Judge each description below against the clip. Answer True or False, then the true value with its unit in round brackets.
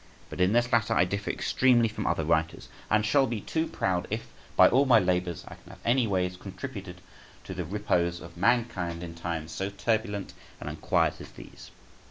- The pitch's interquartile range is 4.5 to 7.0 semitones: True (4.8 semitones)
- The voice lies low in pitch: True (100 Hz)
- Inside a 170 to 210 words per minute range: True (195 wpm)